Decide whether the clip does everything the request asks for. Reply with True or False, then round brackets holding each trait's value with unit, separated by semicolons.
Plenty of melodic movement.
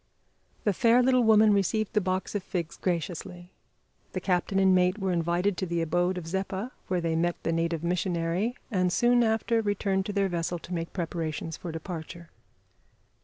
False (3.1 semitones)